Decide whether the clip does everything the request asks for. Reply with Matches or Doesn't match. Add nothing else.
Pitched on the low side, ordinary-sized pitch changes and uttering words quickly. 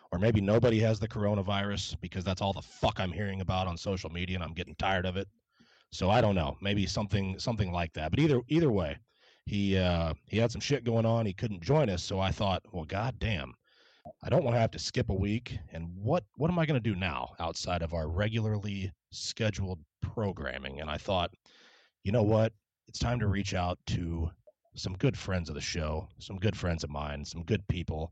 Matches